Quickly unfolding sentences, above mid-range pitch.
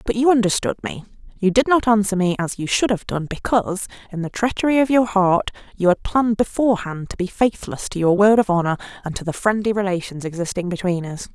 Yes: fast, 215 wpm; high, 200 Hz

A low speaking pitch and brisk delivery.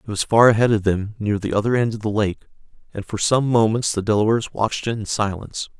Yes: low, 110 Hz; fast, 240 wpm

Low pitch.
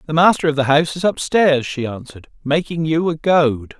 No: medium, 155 Hz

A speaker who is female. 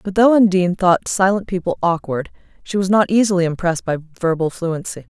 Yes: female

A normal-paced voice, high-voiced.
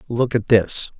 No: average, 180 wpm; low, 115 Hz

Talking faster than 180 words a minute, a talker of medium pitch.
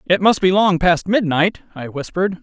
Yes: average, 200 wpm; medium, 180 Hz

